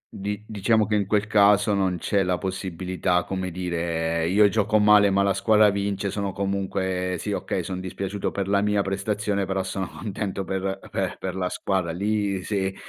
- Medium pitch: No, very low, 95 Hz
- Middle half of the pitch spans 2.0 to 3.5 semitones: No, narrow, 1.6 semitones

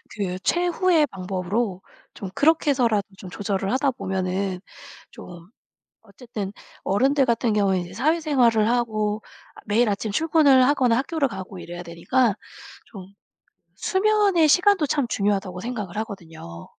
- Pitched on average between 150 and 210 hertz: No, high, 220 Hz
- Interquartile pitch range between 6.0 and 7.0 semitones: Yes, wide, 6.5 semitones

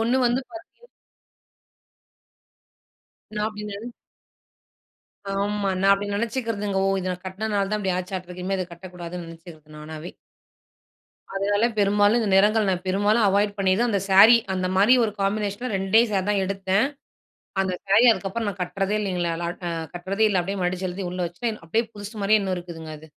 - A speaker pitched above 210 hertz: No, high, 195 Hz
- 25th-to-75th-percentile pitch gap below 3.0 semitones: Yes, narrow, 2.4 semitones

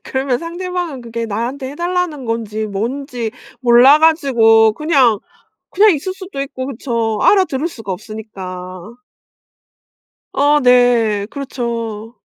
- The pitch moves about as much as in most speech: Yes, average, 4.6 semitones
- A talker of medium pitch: No, high, 245 Hz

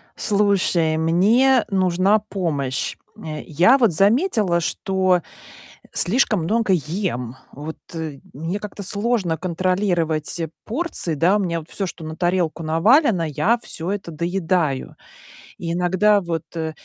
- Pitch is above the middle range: No, medium, 180 Hz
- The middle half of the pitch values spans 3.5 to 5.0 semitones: Yes, average, 4.0 semitones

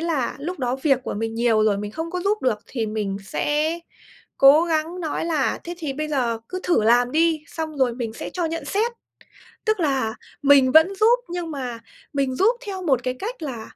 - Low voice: No, very high, 295 Hz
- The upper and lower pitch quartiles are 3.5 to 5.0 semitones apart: No, wide, 5.6 semitones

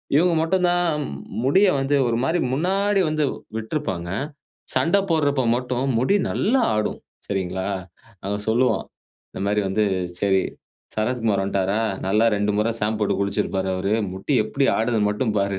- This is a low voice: Yes, low, 115 Hz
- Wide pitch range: Yes, wide, 7.1 semitones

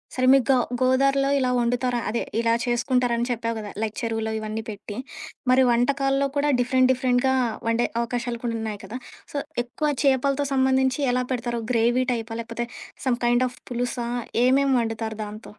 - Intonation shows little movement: Yes, narrow, 2.2 semitones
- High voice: Yes, high, 245 Hz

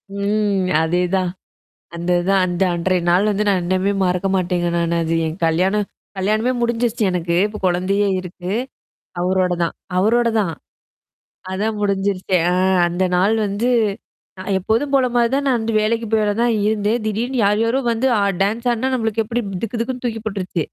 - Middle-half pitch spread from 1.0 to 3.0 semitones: No, average, 3.8 semitones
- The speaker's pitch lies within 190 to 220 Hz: Yes, high, 200 Hz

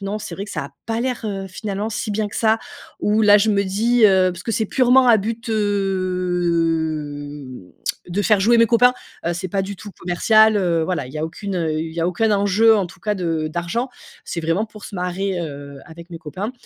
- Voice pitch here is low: No, high, 195 Hz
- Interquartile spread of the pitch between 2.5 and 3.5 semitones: No, average, 4.2 semitones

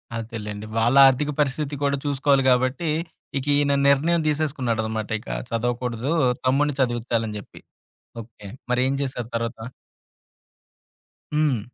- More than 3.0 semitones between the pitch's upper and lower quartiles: Yes, average, 3.7 semitones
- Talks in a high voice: No, low, 125 Hz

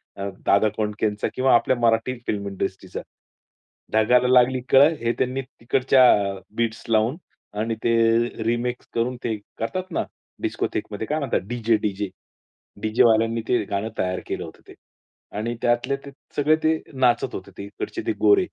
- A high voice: No, low, 115 Hz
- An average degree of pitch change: Yes, average, 3.0 semitones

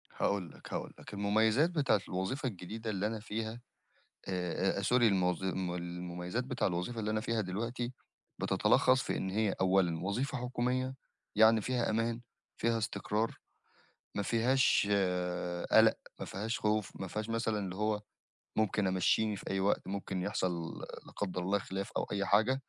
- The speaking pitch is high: No, low, 105 Hz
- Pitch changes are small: No, average, 3.3 semitones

